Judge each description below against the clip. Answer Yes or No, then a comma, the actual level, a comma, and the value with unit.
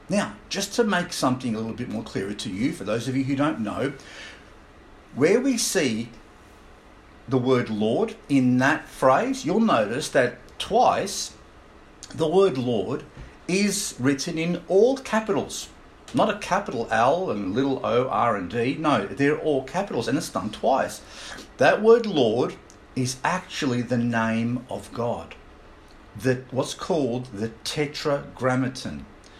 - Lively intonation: Yes, wide, 6.8 semitones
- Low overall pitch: Yes, low, 130 Hz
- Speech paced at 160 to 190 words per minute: No, average, 145 wpm